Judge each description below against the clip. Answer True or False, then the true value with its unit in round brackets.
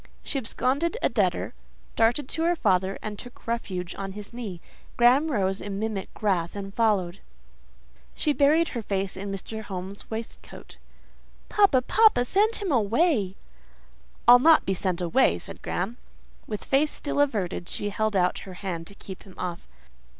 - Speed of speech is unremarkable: True (155 wpm)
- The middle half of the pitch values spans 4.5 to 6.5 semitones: True (5.5 semitones)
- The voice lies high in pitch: True (215 Hz)